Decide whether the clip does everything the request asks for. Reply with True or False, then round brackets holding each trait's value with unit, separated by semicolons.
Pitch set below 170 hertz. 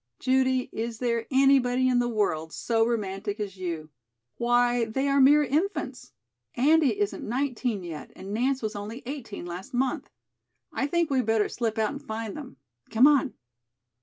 False (245 Hz)